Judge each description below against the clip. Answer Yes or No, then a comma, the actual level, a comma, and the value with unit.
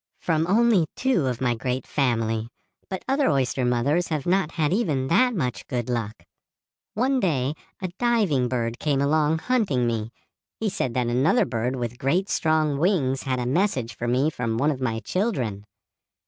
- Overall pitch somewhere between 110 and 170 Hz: Yes, low, 135 Hz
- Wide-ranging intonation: Yes, wide, 6.5 semitones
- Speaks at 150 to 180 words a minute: Yes, average, 175 wpm